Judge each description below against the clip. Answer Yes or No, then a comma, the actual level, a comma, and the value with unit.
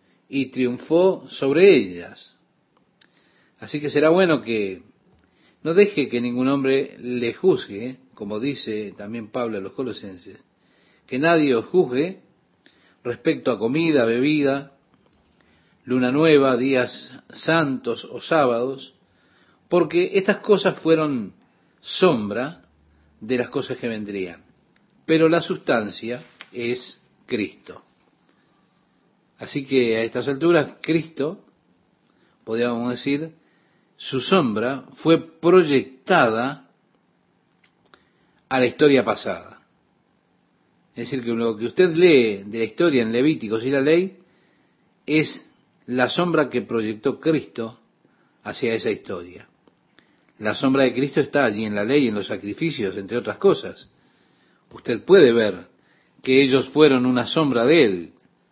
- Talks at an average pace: No, slow, 120 wpm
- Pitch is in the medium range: No, low, 130 Hz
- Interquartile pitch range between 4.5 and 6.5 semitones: Yes, average, 5.2 semitones